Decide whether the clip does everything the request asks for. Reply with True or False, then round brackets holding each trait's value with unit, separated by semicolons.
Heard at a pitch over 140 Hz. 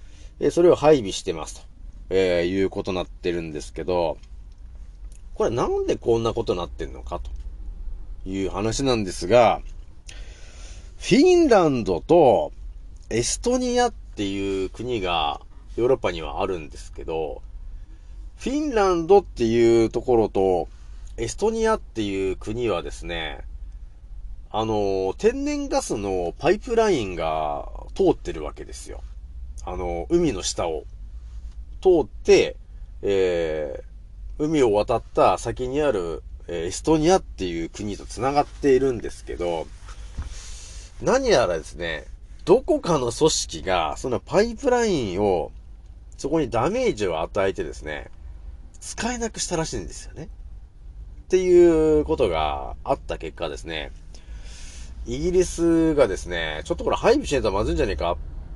False (95 Hz)